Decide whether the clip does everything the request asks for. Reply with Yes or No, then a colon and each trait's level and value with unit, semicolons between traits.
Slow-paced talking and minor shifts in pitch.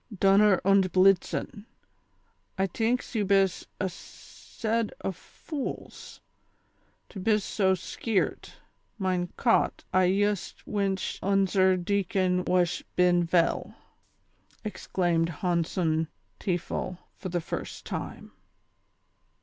Yes: slow, 100 wpm; narrow, 2.1 semitones